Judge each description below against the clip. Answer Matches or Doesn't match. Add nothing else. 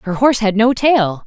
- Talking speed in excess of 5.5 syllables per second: Doesn't match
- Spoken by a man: Doesn't match